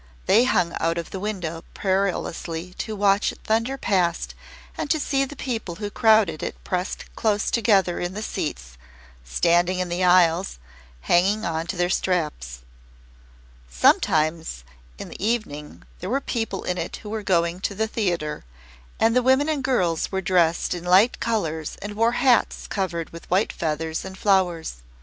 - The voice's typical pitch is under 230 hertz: Yes, medium, 185 Hz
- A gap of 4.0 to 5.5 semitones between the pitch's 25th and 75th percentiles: Yes, average, 4.4 semitones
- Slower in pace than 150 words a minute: No, average, 165 wpm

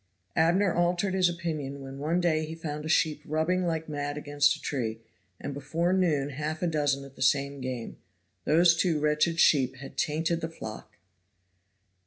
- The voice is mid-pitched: Yes, medium, 155 Hz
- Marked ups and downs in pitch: No, average, 3.1 semitones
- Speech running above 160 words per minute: Yes, average, 175 wpm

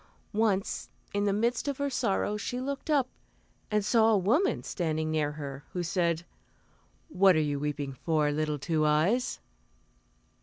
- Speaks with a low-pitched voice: No, medium, 185 Hz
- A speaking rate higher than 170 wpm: No, average, 155 wpm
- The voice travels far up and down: Yes, wide, 6.6 semitones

